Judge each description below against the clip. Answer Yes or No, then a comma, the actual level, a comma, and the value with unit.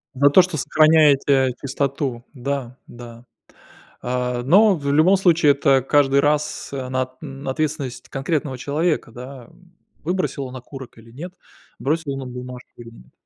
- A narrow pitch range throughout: No, average, 3.4 semitones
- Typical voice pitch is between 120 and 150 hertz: Yes, medium, 140 Hz